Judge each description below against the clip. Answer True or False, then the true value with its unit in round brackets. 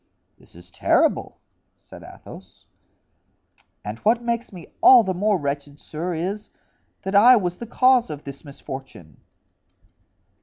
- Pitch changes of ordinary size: False (8.0 semitones)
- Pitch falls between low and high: True (180 Hz)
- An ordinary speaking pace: False (130 wpm)